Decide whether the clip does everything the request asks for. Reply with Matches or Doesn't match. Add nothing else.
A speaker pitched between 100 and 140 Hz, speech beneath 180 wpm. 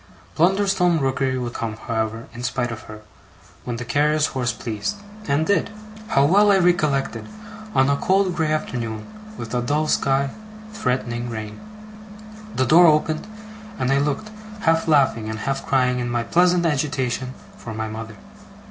Matches